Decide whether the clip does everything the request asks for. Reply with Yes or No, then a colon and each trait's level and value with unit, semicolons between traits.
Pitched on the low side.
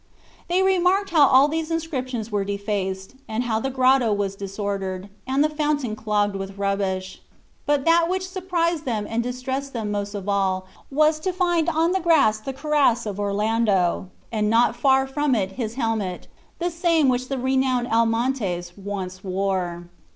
No: high, 235 Hz